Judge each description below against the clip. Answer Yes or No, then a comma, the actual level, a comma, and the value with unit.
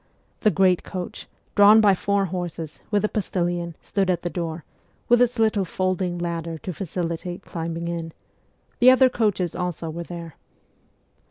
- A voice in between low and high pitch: Yes, medium, 180 Hz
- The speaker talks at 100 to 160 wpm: Yes, average, 155 wpm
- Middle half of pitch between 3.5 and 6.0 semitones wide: No, average, 3.0 semitones